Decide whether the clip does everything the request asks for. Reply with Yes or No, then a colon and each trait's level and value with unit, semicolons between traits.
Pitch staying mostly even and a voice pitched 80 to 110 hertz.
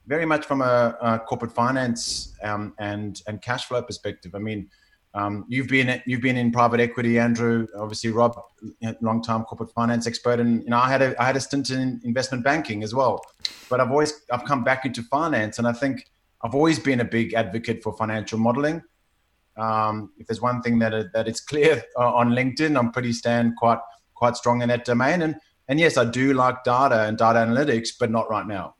No: narrow, 2.3 semitones; low, 120 Hz